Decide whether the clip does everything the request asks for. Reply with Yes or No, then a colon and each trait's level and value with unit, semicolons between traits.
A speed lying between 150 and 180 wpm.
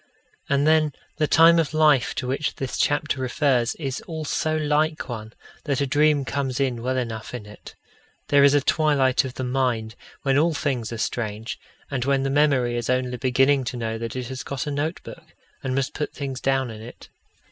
No: average, 200 wpm